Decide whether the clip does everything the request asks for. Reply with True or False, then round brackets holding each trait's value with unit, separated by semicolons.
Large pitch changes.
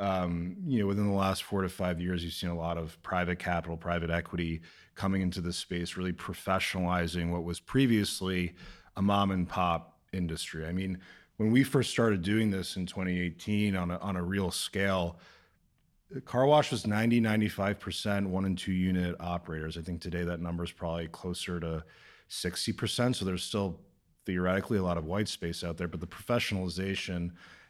False (2.5 semitones)